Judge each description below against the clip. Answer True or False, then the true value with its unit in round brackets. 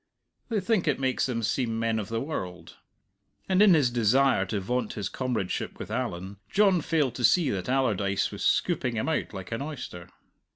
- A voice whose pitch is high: False (125 Hz)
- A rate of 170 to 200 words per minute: True (190 wpm)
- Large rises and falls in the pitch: True (6.3 semitones)